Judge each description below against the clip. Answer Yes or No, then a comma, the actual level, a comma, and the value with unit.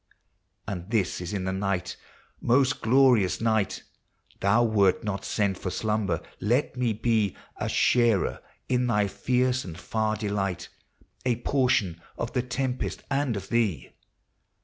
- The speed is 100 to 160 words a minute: Yes, average, 150 wpm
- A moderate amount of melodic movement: Yes, average, 4.1 semitones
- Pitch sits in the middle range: No, low, 110 Hz